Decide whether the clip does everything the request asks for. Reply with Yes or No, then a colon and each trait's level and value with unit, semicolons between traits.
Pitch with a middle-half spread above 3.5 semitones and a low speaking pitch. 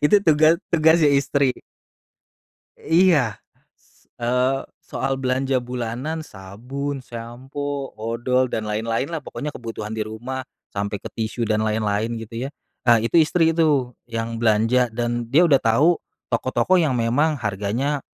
Yes: average, 4.0 semitones; low, 125 Hz